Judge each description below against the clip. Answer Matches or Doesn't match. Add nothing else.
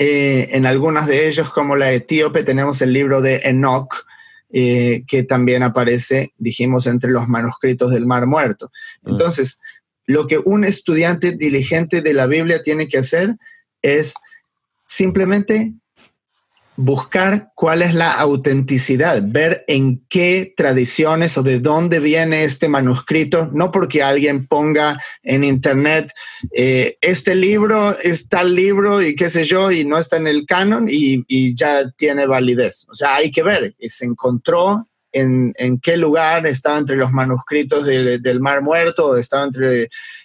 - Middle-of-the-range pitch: Matches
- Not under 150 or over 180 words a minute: Matches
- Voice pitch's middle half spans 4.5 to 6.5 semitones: Matches